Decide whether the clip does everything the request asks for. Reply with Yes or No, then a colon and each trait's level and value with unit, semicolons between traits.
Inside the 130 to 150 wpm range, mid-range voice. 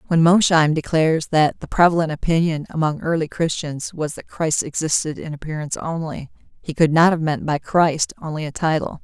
No: average, 180 wpm; medium, 160 Hz